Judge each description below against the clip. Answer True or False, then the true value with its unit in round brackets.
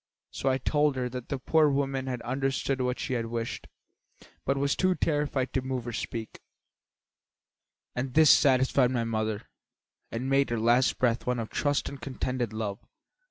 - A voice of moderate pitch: False (130 Hz)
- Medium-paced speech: True (165 wpm)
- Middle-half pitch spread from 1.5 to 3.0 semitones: True (2.5 semitones)